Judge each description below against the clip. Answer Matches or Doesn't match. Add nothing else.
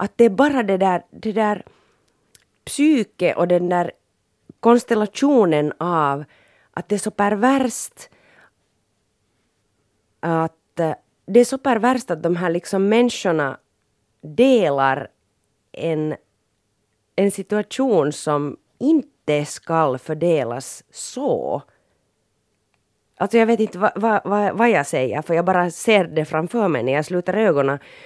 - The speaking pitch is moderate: Matches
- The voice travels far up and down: Matches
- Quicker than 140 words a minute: Doesn't match